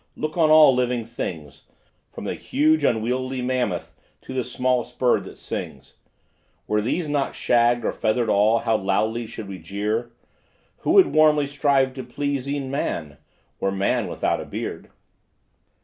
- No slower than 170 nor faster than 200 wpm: No, average, 155 wpm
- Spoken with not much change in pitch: No, average, 4.3 semitones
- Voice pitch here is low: Yes, low, 125 Hz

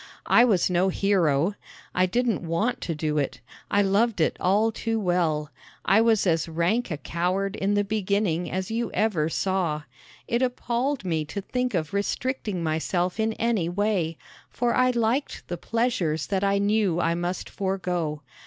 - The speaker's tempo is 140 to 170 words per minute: Yes, average, 165 wpm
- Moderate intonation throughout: Yes, average, 4.6 semitones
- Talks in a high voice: Yes, high, 195 Hz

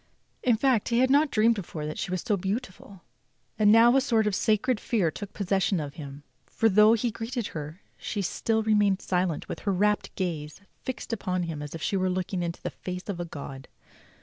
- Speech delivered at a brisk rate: Yes, fast, 210 wpm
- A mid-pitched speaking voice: No, high, 200 Hz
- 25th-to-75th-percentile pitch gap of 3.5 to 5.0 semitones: Yes, average, 4.3 semitones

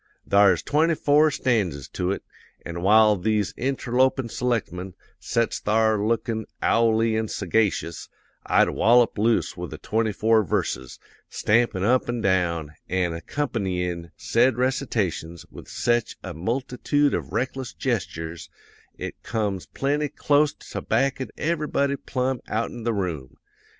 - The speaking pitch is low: Yes, low, 110 Hz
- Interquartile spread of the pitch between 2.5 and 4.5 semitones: No, wide, 5.4 semitones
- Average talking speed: No, slow, 130 wpm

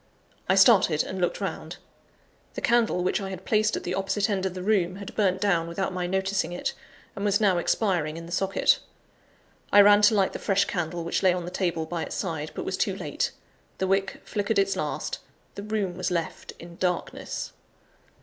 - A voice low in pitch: No, high, 190 Hz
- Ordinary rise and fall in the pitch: No, narrow, 2.3 semitones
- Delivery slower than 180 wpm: No, fast, 205 wpm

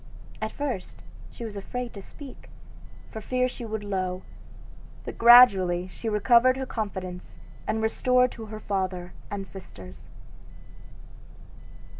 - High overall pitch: Yes, high, 215 Hz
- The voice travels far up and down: No, average, 4.5 semitones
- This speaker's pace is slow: Yes, slow, 130 wpm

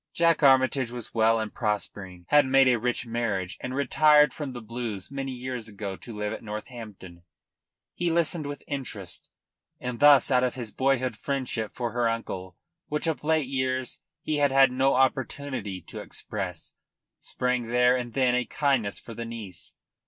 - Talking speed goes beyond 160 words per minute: Yes, average, 170 wpm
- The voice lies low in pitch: Yes, low, 125 Hz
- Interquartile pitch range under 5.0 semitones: Yes, average, 3.5 semitones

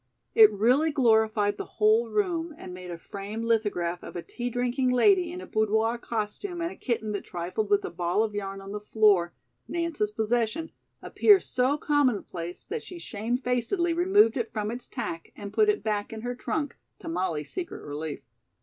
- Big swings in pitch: Yes, wide, 6.1 semitones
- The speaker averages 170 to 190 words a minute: Yes, average, 185 wpm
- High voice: Yes, high, 225 Hz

